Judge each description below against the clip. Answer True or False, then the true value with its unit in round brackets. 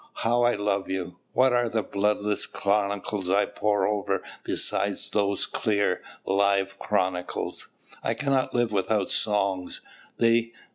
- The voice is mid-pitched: False (105 Hz)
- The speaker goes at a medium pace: False (130 wpm)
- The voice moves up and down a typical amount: False (2.2 semitones)